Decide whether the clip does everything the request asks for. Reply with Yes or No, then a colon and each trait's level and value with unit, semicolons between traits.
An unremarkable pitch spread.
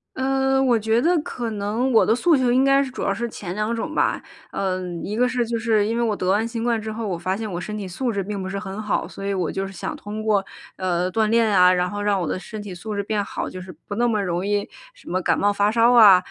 Yes: average, 3.3 semitones